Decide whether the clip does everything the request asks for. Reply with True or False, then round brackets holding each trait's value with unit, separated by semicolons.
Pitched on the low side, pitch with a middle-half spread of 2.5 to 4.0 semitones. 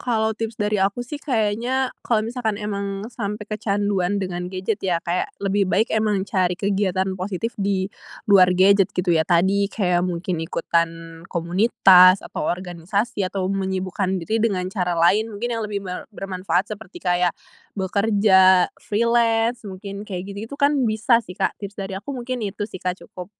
False (200 Hz; 2.9 semitones)